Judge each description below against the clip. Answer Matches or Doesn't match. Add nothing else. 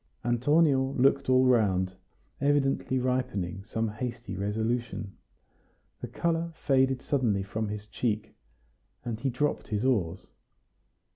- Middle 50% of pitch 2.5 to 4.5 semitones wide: Matches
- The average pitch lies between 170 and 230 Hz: Doesn't match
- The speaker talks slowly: Matches